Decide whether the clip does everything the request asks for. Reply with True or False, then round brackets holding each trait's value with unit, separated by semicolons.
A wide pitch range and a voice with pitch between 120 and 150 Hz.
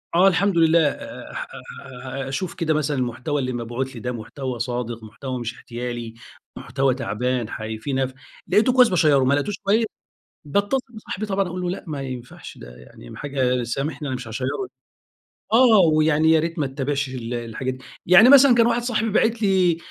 True (6.6 semitones; 140 Hz)